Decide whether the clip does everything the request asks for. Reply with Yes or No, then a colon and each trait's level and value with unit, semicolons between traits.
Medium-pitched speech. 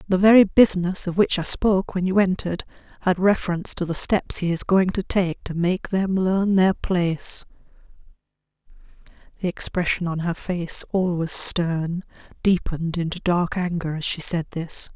Yes: medium, 180 Hz